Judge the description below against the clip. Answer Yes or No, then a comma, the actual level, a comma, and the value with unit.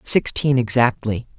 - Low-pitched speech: Yes, low, 125 Hz